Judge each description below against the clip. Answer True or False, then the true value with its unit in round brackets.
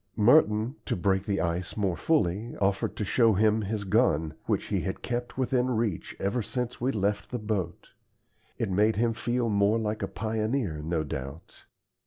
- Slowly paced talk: False (175 wpm)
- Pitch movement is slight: False (3.5 semitones)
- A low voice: True (105 Hz)